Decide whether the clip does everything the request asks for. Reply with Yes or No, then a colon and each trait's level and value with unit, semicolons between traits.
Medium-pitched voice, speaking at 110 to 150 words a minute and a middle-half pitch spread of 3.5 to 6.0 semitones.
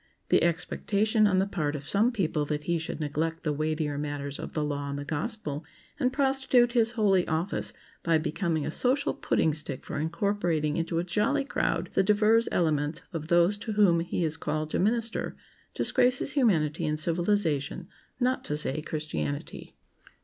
No: medium, 170 Hz; average, 170 wpm; wide, 5.6 semitones